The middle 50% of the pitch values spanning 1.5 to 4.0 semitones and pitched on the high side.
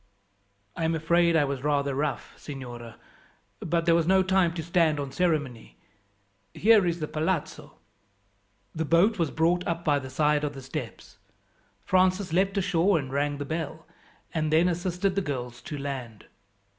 No: average, 3.7 semitones; medium, 160 Hz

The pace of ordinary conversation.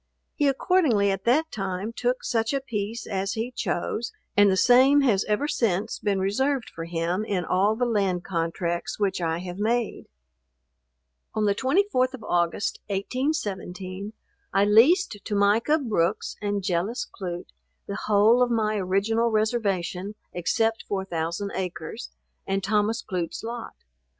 Yes: average, 145 wpm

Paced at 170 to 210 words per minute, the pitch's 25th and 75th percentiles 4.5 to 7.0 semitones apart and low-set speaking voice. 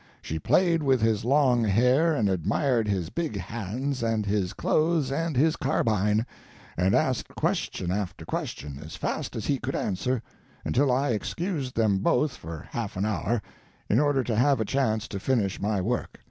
Yes: average, 175 wpm; average, 5.3 semitones; low, 115 Hz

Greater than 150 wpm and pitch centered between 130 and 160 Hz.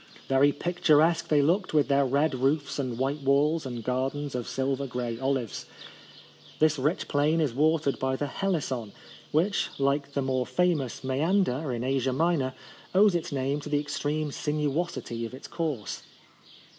Yes: average, 160 wpm; medium, 140 Hz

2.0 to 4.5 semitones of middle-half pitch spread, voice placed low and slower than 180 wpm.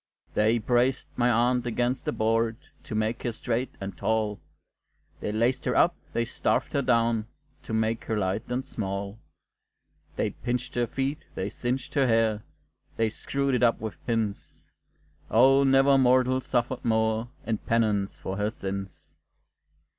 Yes: narrow, 2.4 semitones; low, 115 Hz; average, 155 wpm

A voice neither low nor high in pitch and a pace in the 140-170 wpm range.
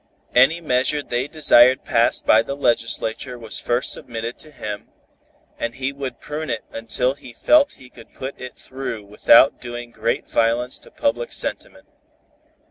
No: low, 125 Hz; average, 160 wpm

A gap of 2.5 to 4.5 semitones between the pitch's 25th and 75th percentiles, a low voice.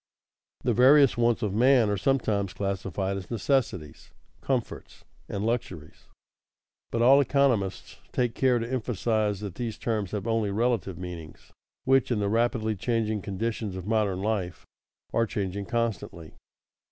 Yes: average, 3.5 semitones; low, 110 Hz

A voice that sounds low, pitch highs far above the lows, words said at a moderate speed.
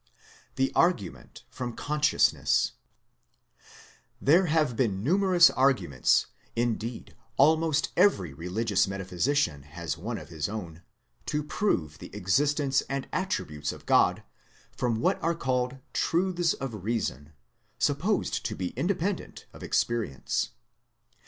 No: low, 125 Hz; wide, 8.9 semitones; slow, 110 wpm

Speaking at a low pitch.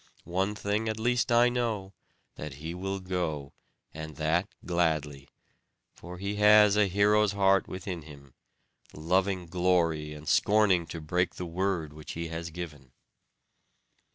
Yes: very low, 90 Hz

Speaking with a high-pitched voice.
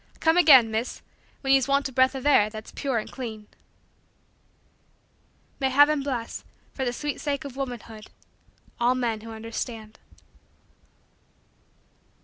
Yes: very high, 255 Hz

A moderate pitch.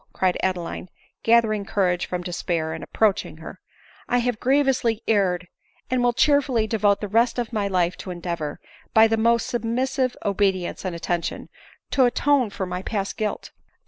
No: high, 210 Hz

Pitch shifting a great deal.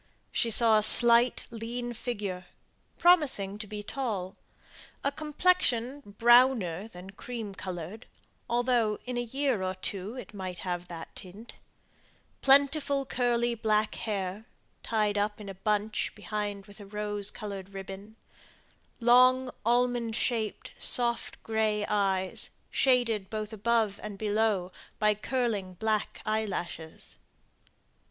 No: average, 3.3 semitones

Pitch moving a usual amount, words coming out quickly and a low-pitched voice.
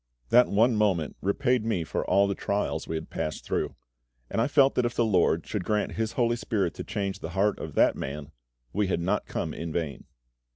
Yes: average, 4.8 semitones; fast, 215 wpm; low, 100 Hz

